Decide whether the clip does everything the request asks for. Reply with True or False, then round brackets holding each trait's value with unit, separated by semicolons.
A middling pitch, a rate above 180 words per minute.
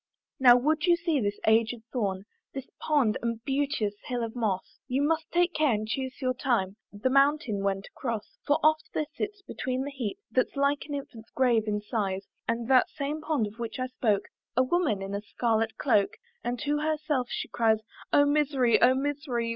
False (255 Hz; 195 wpm)